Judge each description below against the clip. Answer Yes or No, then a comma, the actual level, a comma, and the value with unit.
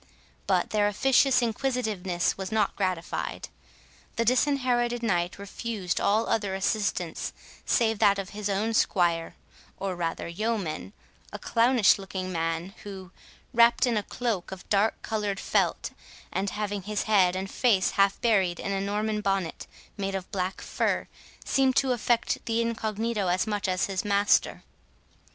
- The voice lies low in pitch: No, high, 205 Hz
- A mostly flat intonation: No, average, 3.1 semitones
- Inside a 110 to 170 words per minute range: Yes, average, 145 wpm